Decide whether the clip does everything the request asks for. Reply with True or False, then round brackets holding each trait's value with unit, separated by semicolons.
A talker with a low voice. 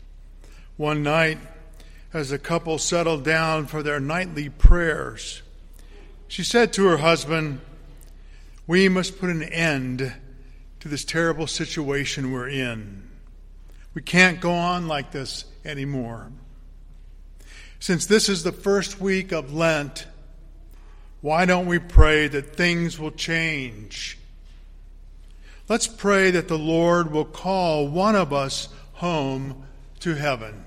False (150 Hz)